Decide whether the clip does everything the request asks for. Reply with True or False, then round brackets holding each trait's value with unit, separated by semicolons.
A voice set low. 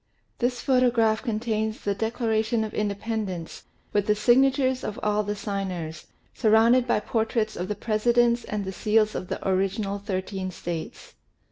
False (215 Hz)